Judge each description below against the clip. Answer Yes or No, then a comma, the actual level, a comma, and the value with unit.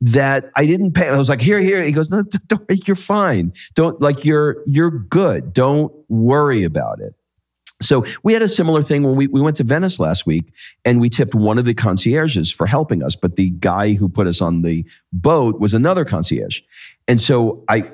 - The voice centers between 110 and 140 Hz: Yes, low, 135 Hz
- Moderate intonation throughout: No, wide, 7.0 semitones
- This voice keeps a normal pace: No, fast, 215 wpm